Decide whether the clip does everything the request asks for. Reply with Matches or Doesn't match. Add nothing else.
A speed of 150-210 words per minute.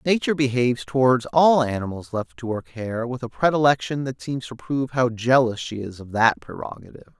Matches